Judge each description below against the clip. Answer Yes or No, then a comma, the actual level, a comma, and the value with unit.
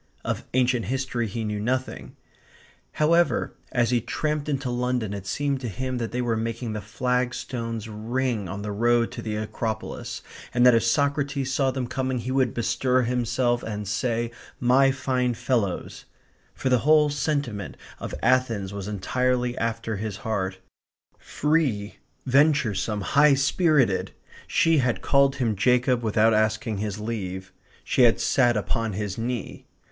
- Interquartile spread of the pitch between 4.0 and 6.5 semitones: No, average, 3.2 semitones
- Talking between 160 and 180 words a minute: No, average, 150 wpm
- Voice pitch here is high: No, low, 120 Hz